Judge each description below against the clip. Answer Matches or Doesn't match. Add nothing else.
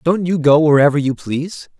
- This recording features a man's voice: Matches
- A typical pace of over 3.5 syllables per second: Matches